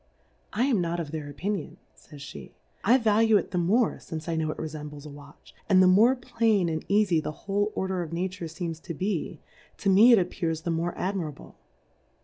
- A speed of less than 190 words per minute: No, average, 195 wpm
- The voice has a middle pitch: Yes, medium, 180 Hz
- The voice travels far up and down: No, average, 4.4 semitones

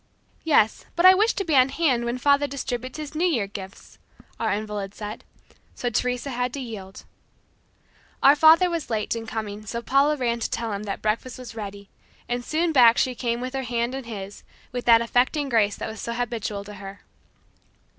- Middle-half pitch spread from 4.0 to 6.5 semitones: Yes, average, 4.3 semitones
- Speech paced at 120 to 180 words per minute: No, average, 195 wpm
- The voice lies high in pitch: Yes, high, 240 Hz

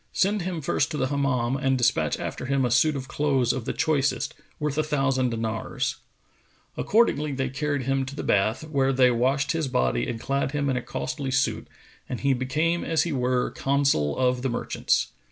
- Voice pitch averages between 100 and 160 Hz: Yes, low, 135 Hz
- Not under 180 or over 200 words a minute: Yes, average, 195 wpm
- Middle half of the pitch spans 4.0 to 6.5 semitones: No, narrow, 2.5 semitones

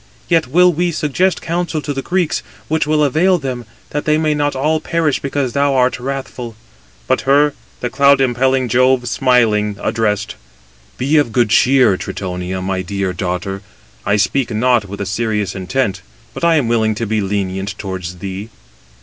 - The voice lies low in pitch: Yes, low, 125 Hz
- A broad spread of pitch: Yes, wide, 6.1 semitones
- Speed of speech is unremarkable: Yes, average, 165 wpm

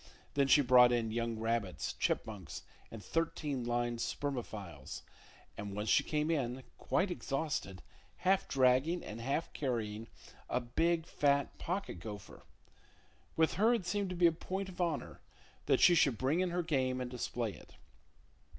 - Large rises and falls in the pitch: Yes, wide, 6.1 semitones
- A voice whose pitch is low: Yes, low, 130 Hz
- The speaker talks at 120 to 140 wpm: No, average, 155 wpm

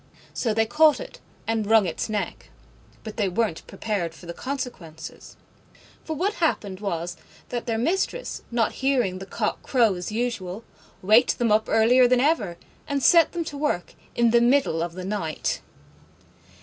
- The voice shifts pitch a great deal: Yes, wide, 5.7 semitones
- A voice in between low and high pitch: No, high, 225 Hz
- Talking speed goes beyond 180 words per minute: No, average, 165 wpm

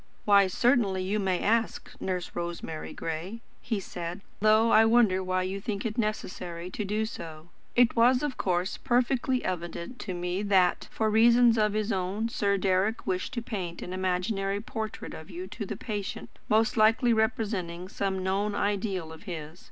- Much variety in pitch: No, average, 3.4 semitones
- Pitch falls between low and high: No, high, 200 Hz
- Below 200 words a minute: Yes, average, 165 wpm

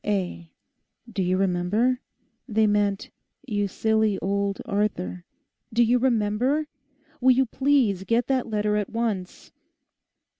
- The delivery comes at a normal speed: No, slow, 110 wpm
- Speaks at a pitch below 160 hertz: No, high, 210 Hz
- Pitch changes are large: No, average, 3.5 semitones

